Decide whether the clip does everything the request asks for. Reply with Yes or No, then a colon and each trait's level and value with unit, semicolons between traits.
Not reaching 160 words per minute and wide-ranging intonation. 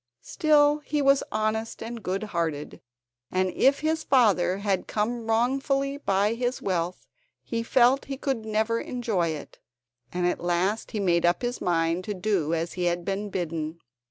No: average, 165 wpm; wide, 5.7 semitones